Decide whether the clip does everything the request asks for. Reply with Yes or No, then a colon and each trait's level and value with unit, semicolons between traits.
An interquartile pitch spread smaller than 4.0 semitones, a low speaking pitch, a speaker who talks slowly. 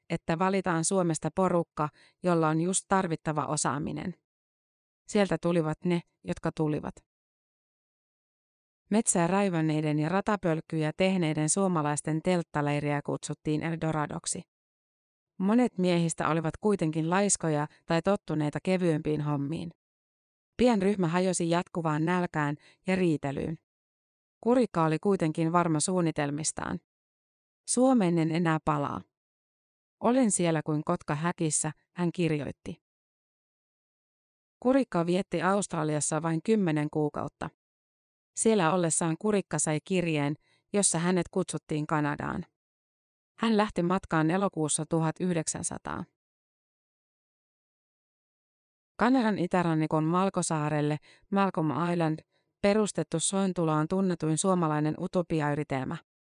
No: average, 3.3 semitones; medium, 165 Hz; slow, 90 wpm